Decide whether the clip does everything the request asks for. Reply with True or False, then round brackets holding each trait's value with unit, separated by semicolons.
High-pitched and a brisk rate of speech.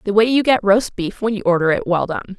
True (205 Hz; 300 wpm)